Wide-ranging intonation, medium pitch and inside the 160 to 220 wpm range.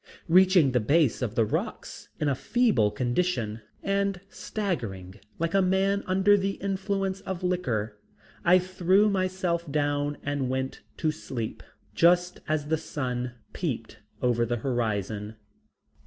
No: wide, 7.5 semitones; medium, 155 Hz; slow, 135 wpm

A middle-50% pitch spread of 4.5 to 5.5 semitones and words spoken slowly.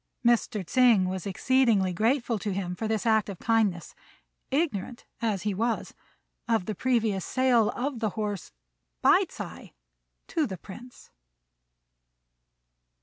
No: average, 3.6 semitones; slow, 130 wpm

